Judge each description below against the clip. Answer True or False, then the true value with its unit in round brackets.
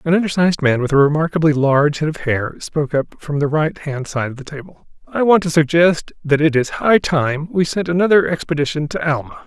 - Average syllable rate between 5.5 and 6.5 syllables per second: True (5.7 syllables/s)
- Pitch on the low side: False (155 Hz)